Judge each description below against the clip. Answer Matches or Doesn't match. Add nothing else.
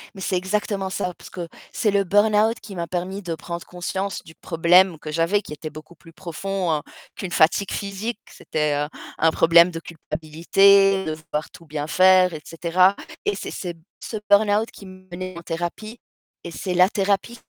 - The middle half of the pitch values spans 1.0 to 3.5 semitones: Matches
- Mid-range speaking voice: Matches